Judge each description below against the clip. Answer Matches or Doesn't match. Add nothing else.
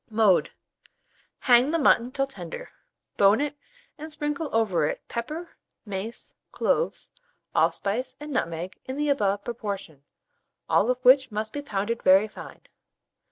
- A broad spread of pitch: Matches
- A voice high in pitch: Matches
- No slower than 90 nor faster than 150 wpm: Matches